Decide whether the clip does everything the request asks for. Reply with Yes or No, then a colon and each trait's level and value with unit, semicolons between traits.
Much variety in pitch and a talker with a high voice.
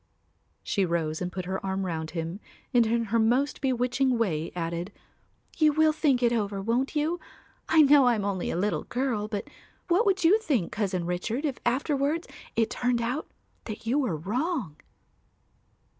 Yes: wide, 6.5 semitones; high, 230 Hz